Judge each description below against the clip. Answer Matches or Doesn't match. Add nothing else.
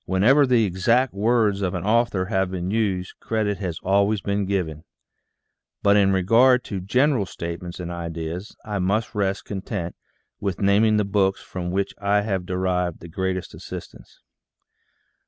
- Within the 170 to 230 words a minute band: Doesn't match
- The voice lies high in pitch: Doesn't match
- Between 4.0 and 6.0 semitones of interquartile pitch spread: Doesn't match